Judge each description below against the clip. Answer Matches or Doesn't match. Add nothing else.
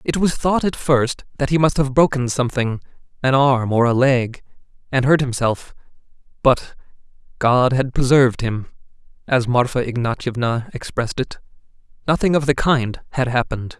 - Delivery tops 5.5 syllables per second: Doesn't match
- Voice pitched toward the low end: Matches